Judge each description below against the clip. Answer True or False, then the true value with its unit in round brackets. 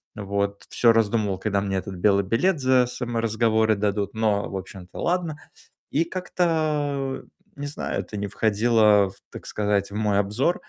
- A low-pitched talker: True (110 Hz)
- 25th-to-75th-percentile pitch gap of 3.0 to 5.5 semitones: True (4.5 semitones)